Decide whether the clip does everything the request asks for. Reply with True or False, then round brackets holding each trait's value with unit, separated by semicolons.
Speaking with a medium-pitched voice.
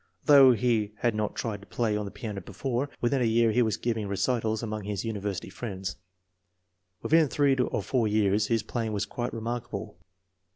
False (110 Hz)